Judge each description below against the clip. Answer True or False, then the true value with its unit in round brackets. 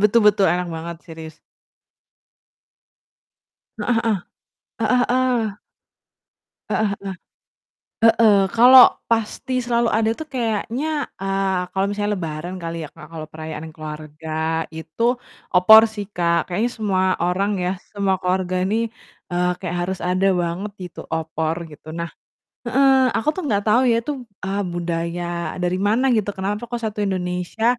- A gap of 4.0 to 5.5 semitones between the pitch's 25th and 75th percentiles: True (4.5 semitones)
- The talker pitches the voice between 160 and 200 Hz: True (190 Hz)